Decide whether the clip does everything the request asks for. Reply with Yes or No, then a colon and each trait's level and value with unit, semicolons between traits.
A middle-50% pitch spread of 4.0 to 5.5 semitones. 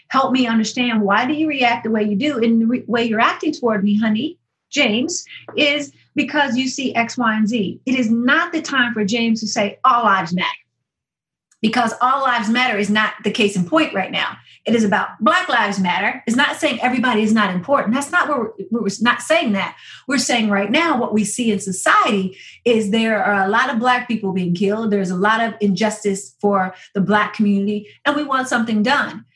No: average, 3.6 semitones